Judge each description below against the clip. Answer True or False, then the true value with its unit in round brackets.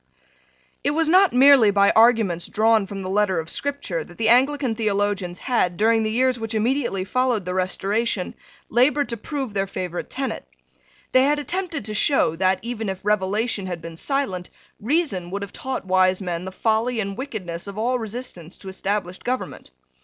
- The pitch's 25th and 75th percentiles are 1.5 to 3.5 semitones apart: False (5.1 semitones)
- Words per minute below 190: True (175 wpm)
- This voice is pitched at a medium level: False (215 Hz)